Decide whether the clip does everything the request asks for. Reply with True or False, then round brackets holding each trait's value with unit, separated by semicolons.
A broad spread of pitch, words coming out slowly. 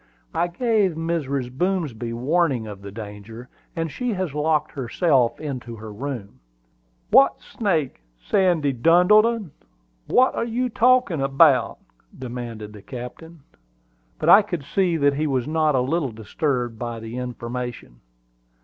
True (6.3 semitones; 130 wpm)